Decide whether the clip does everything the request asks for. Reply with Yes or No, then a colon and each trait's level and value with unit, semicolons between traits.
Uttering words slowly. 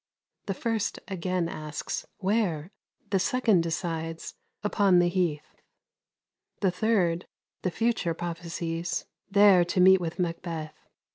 Yes: slow, 115 wpm